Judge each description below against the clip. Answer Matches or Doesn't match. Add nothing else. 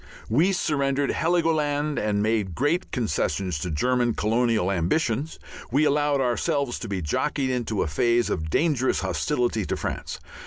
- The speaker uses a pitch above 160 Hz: Doesn't match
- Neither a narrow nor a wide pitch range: Doesn't match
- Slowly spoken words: Doesn't match